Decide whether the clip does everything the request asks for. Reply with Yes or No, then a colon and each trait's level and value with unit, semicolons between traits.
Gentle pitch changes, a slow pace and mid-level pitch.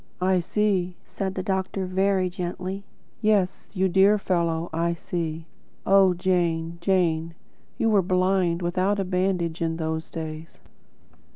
Yes: narrow, 2.3 semitones; slow, 130 wpm; medium, 180 Hz